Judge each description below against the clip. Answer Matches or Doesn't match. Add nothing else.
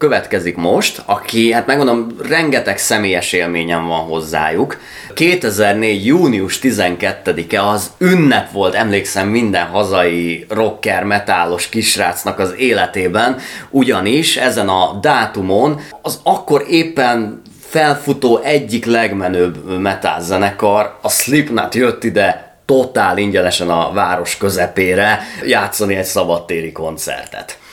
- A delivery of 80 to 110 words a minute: Matches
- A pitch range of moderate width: Matches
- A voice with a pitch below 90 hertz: Doesn't match